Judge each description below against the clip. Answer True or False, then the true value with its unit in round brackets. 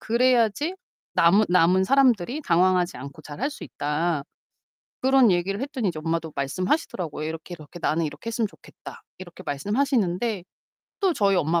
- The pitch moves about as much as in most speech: False (6.3 semitones)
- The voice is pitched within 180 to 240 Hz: True (185 Hz)